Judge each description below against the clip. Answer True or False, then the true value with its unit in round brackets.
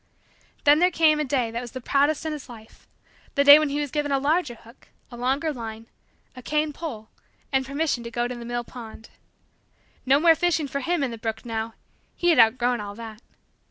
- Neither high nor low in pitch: False (265 Hz)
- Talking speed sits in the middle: False (215 wpm)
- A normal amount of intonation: True (4.4 semitones)